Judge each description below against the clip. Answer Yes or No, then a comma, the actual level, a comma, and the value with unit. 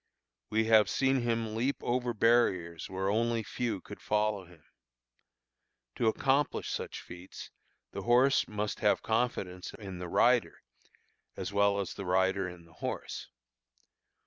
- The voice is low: Yes, low, 105 Hz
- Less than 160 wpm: Yes, average, 140 wpm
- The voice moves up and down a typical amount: Yes, average, 4.0 semitones